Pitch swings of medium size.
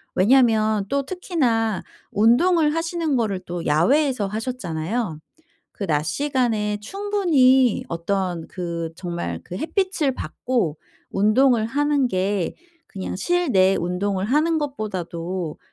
No: wide, 7.2 semitones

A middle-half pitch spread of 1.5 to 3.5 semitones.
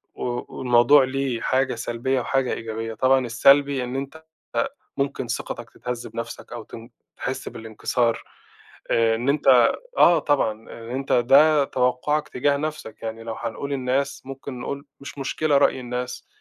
Yes: average, 3.0 semitones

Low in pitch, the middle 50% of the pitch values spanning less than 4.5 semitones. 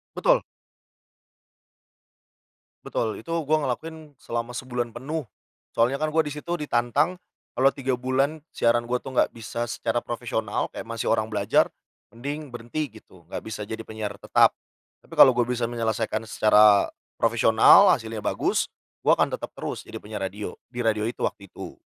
Yes: low, 120 Hz; average, 3.5 semitones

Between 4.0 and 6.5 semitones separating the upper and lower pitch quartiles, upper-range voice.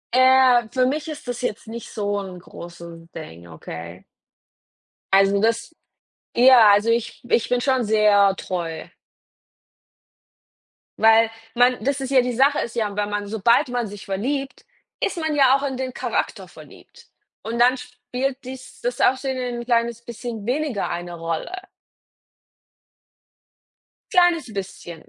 Yes: average, 4.3 semitones; high, 235 Hz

